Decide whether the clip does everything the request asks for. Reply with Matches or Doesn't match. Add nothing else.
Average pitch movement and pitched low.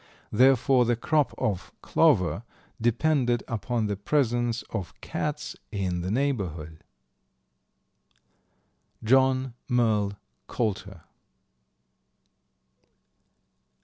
Matches